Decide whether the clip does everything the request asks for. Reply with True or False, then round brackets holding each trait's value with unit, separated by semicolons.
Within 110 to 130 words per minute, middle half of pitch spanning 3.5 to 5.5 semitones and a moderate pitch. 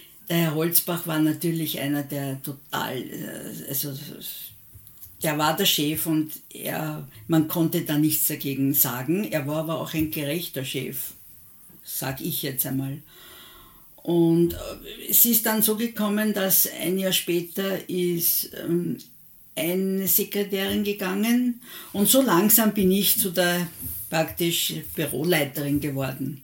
True (125 wpm; 4.5 semitones; 165 Hz)